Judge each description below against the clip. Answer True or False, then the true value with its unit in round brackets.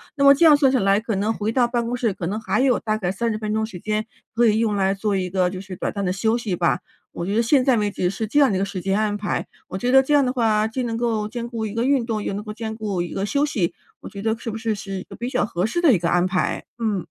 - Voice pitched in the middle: False (215 Hz)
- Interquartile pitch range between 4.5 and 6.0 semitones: False (3.3 semitones)